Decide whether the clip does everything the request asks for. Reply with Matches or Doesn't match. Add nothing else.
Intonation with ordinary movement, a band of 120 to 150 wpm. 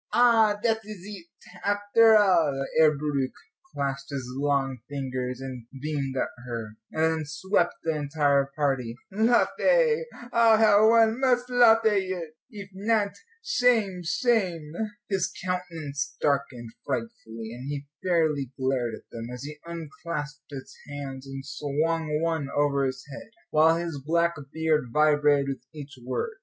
Doesn't match